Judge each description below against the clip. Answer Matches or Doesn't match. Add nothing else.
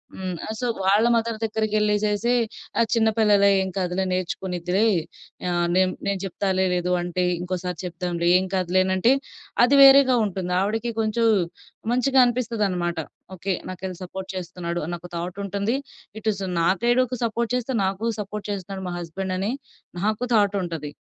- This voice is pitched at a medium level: Doesn't match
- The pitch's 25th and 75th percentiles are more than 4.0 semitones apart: Doesn't match